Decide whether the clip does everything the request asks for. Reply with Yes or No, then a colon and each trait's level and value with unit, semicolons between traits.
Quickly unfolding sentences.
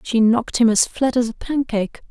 Yes: fast, 230 wpm